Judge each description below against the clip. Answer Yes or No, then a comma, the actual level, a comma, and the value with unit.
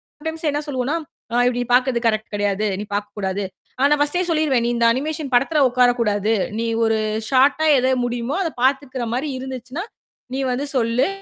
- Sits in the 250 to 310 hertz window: Yes, very high, 255 Hz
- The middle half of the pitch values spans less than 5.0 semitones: Yes, average, 3.8 semitones